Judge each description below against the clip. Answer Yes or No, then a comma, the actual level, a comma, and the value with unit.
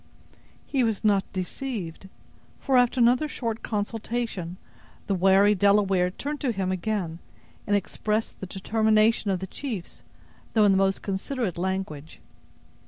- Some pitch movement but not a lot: Yes, average, 3.2 semitones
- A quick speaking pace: No, slow, 135 wpm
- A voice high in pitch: Yes, high, 205 Hz